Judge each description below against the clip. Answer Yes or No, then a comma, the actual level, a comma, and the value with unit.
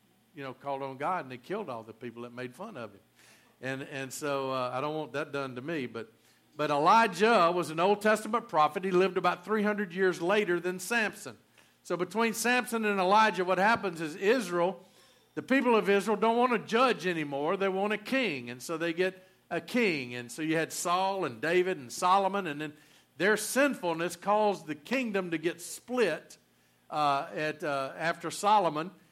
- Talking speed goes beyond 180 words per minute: Yes, average, 195 wpm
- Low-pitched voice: No, medium, 175 Hz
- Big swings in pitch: Yes, wide, 5.8 semitones